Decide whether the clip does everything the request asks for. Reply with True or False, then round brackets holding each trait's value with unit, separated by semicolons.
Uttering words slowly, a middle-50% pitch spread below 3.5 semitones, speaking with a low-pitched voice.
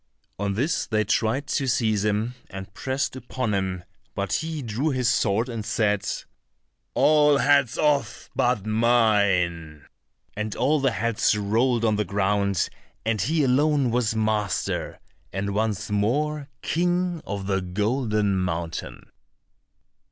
False (130 wpm; 4.6 semitones; 110 Hz)